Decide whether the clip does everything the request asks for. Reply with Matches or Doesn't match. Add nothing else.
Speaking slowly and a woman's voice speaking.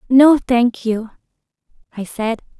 Matches